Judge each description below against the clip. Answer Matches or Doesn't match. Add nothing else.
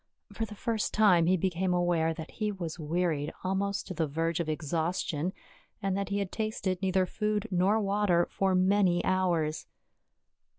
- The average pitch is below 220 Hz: Matches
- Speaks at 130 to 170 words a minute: Matches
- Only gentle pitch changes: Doesn't match